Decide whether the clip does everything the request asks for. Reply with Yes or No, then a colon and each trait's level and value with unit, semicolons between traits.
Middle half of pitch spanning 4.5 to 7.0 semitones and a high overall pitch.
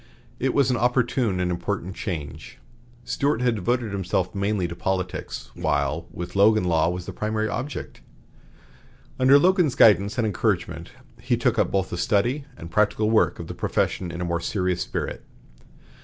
No: average, 5.2 semitones; low, 100 Hz